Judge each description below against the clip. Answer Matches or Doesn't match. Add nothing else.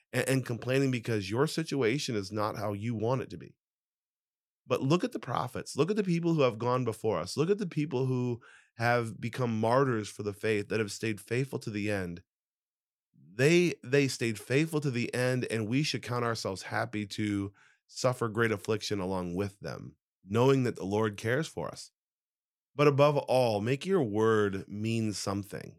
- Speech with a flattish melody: Doesn't match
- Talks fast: Doesn't match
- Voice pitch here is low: Matches